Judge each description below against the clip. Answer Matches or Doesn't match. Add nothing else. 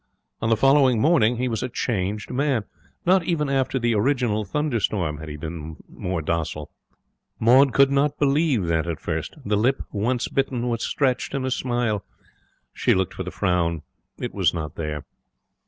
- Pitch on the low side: Matches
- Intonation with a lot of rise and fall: Matches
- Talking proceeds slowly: Doesn't match